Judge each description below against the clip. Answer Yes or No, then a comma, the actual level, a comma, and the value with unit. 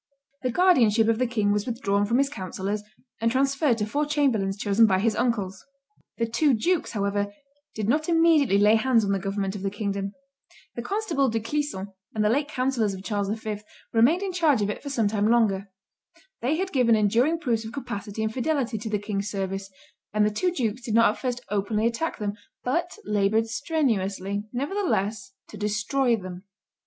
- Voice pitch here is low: No, high, 225 Hz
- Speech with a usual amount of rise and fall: Yes, average, 4.8 semitones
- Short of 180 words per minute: No, average, 190 wpm